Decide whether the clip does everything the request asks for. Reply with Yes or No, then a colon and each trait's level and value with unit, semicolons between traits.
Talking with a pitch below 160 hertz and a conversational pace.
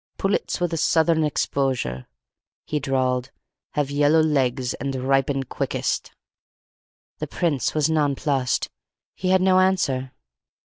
No: medium, 140 Hz; slow, 120 wpm